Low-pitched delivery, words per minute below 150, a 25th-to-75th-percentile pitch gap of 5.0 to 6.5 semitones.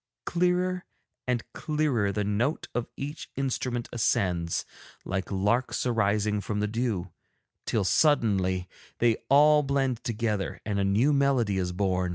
Yes: low, 115 Hz; slow, 135 wpm; wide, 5.6 semitones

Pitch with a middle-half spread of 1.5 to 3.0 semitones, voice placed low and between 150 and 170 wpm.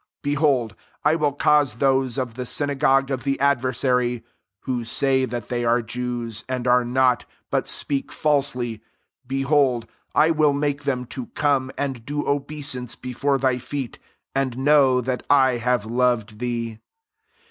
Yes: narrow, 2.6 semitones; low, 130 Hz; average, 155 wpm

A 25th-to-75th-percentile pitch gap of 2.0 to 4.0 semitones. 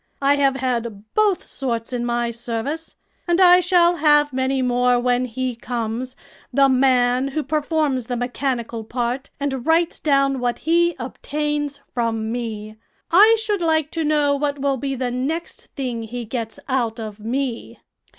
Yes: average, 3.6 semitones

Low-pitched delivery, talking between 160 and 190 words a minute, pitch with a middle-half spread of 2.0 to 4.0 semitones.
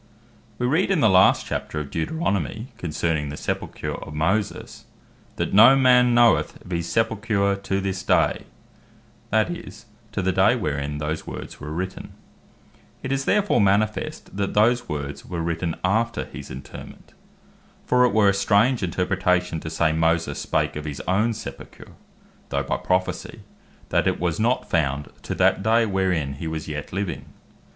No: very low, 95 Hz; average, 165 wpm; wide, 5.6 semitones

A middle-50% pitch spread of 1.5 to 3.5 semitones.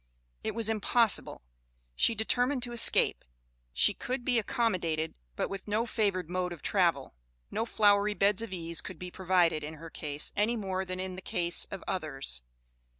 No: average, 4.5 semitones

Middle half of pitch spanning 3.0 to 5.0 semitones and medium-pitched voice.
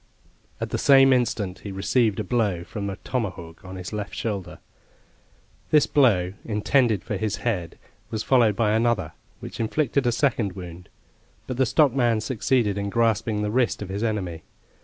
No: average, 3.7 semitones; low, 110 Hz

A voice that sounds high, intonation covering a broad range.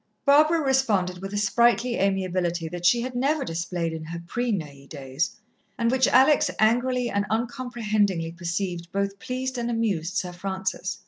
Yes: high, 200 Hz; wide, 5.9 semitones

